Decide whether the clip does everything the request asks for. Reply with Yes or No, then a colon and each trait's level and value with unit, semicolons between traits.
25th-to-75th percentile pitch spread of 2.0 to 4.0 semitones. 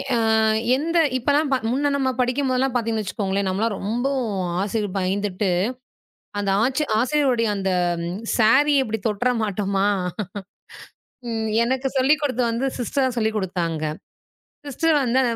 No: average, 4.8 semitones